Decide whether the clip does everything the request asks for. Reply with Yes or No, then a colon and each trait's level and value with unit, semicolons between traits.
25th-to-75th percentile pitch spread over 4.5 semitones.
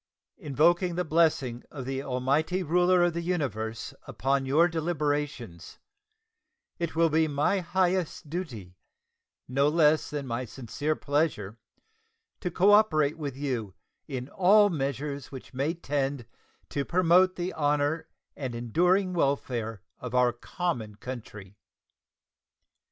Yes: average, 5.1 semitones